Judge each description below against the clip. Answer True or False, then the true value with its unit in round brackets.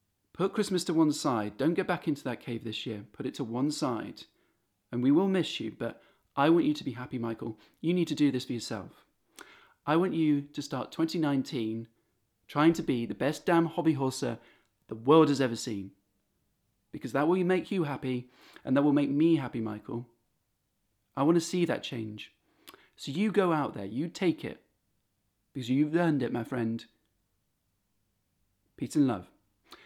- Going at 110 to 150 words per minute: False (185 wpm)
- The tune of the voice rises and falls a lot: True (6.5 semitones)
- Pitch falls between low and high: False (130 Hz)